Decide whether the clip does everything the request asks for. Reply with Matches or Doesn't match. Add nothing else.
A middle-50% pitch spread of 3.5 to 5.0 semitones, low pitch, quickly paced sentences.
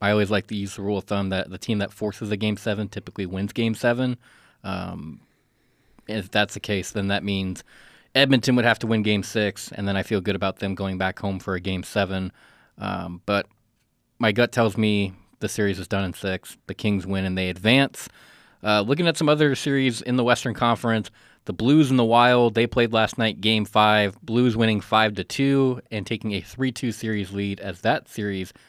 Doesn't match